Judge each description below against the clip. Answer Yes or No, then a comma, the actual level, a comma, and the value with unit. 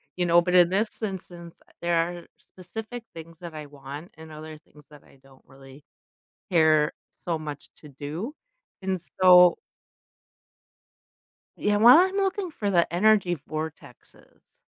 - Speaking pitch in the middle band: Yes, medium, 170 Hz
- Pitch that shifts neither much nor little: Yes, average, 3.8 semitones